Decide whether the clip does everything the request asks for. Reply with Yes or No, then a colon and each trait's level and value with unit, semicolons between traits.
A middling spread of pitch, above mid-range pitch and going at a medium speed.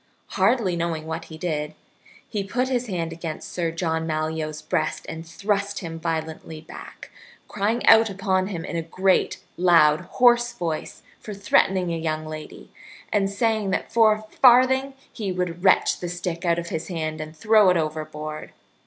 No: average, 4.2 semitones; medium, 175 Hz; average, 170 wpm